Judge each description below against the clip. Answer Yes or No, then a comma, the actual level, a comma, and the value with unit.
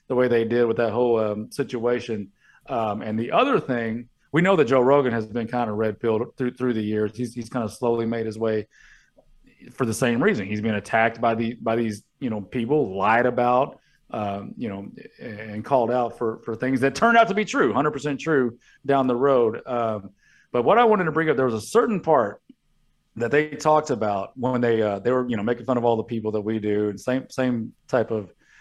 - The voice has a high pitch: No, low, 120 Hz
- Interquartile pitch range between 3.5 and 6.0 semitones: No, average, 2.9 semitones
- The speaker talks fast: Yes, fast, 235 wpm